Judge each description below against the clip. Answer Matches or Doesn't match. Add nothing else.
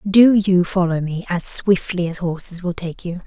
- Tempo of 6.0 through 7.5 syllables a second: Doesn't match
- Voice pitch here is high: Doesn't match